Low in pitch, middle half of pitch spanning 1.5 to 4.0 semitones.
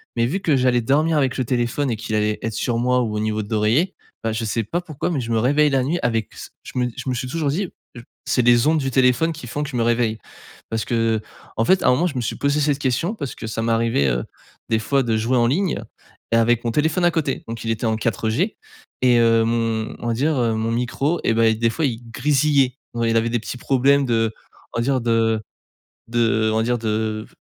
Yes: low, 120 Hz; average, 3.6 semitones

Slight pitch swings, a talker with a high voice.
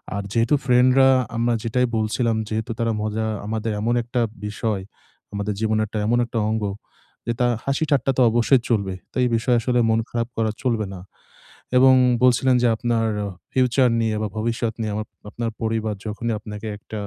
No: narrow, 2.1 semitones; low, 115 Hz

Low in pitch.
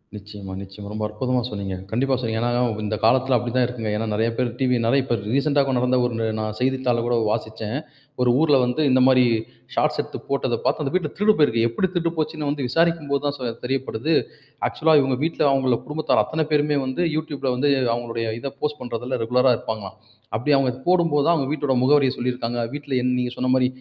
Yes: low, 130 Hz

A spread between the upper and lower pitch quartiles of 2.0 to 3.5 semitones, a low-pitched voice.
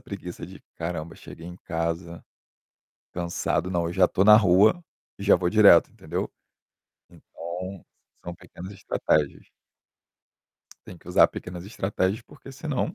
Yes: average, 2.7 semitones; very low, 90 Hz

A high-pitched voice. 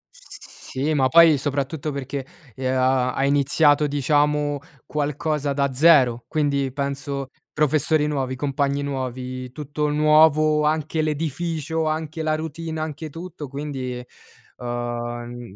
No: medium, 145 Hz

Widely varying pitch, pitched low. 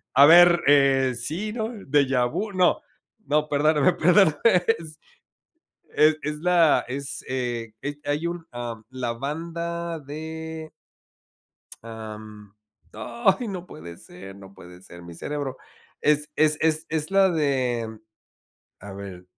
No: wide, 5.7 semitones; medium, 150 Hz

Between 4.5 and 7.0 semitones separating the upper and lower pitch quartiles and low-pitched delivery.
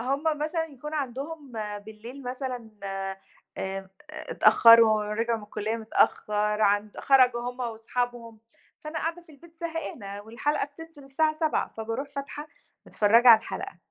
No: average, 5.1 semitones; high, 245 Hz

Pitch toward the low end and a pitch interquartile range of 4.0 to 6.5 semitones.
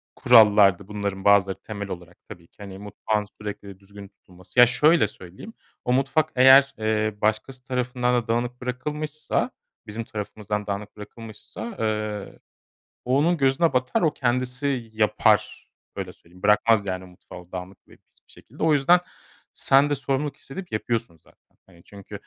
Yes: low, 110 Hz; average, 4.6 semitones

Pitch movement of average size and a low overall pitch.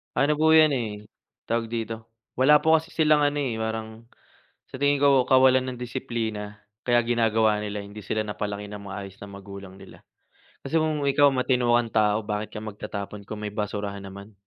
Yes: average, 4.0 semitones; low, 110 Hz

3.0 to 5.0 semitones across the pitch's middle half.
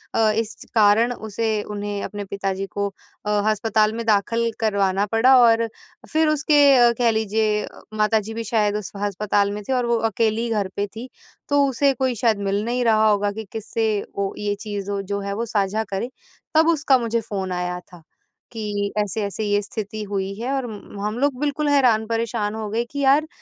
No: narrow, 2.5 semitones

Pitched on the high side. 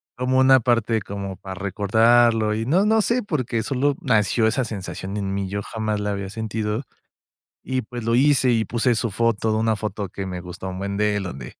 No: low, 110 Hz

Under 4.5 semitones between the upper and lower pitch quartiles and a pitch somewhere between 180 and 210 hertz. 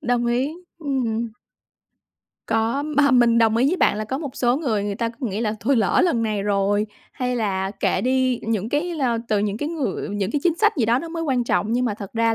No: average, 4.0 semitones; high, 235 Hz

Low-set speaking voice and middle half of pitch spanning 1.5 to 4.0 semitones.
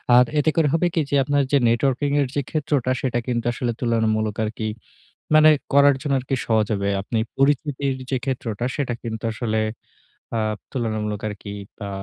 No: low, 125 Hz; average, 4.4 semitones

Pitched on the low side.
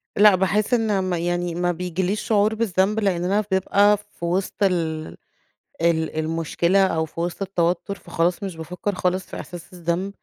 No: medium, 180 Hz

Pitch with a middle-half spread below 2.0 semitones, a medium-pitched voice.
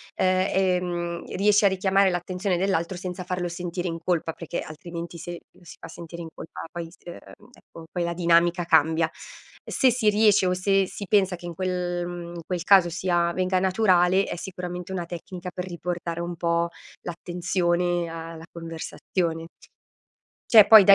Yes: narrow, 1.5 semitones; medium, 175 Hz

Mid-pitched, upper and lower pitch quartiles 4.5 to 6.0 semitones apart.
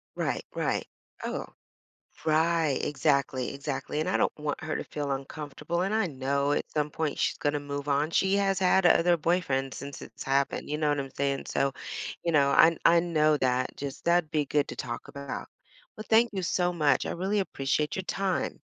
No: medium, 150 Hz; average, 3.6 semitones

